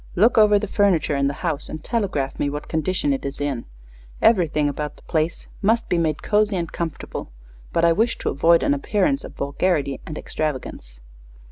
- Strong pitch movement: Yes, wide, 5.9 semitones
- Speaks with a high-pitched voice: No, medium, 165 Hz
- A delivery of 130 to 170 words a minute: No, average, 190 wpm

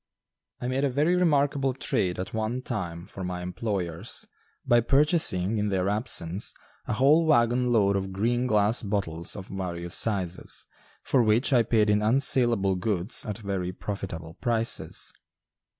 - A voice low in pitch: Yes, low, 105 Hz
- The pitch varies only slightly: No, average, 4.7 semitones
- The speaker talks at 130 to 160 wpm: Yes, average, 150 wpm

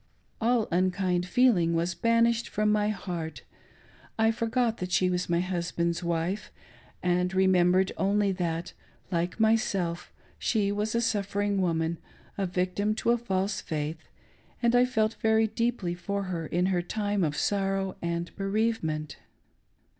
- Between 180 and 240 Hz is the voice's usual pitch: Yes, high, 190 Hz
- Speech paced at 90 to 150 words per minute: Yes, average, 145 wpm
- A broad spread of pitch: No, average, 3.7 semitones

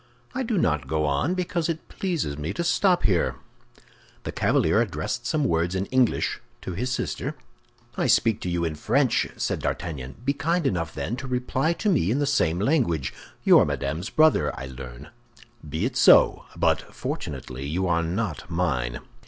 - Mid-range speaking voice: No, low, 100 Hz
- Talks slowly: No, average, 175 wpm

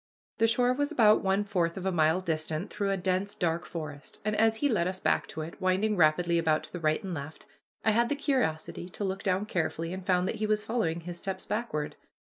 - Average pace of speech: No, fast, 235 wpm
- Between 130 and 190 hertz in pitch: Yes, medium, 185 Hz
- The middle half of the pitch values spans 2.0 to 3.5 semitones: No, average, 4.2 semitones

